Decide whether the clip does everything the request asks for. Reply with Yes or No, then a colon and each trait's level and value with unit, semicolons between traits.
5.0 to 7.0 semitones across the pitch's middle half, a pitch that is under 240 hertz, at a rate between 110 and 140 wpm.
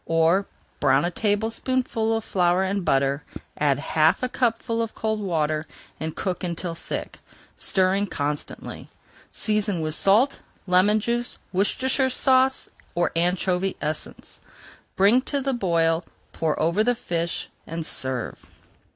Yes: wide, 5.4 semitones; high, 190 Hz; slow, 135 wpm